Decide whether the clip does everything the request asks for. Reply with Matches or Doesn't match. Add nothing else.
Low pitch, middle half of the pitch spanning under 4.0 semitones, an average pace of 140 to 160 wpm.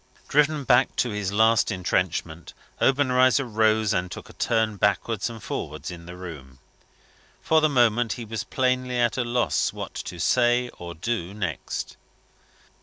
Doesn't match